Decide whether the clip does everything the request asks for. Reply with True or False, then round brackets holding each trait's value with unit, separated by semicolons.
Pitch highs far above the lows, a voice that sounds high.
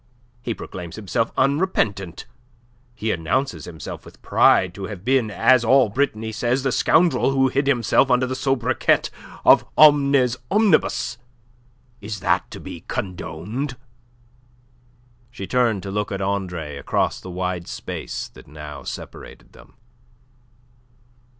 False (5.9 semitones; 115 Hz)